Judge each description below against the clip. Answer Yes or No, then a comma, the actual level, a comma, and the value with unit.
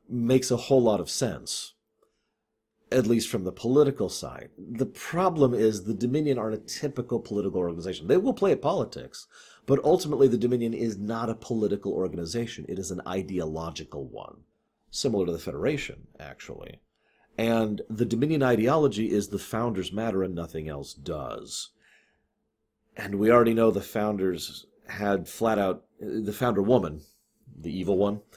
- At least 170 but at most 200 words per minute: No, average, 155 wpm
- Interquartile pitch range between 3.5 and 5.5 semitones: Yes, average, 4.2 semitones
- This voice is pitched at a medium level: No, low, 110 Hz